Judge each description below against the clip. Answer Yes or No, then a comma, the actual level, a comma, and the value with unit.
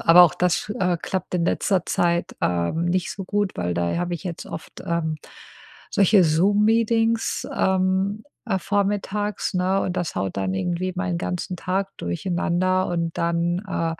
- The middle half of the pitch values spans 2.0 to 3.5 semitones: Yes, narrow, 2.5 semitones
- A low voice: No, medium, 180 Hz